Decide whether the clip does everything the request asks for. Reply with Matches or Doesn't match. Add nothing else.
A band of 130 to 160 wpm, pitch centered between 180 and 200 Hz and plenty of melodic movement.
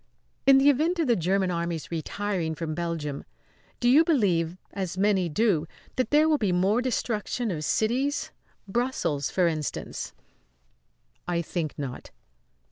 Matches